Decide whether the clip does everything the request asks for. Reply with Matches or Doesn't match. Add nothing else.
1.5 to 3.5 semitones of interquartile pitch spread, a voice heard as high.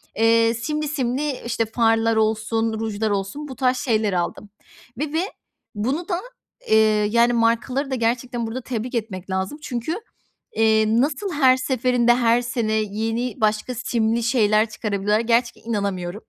Matches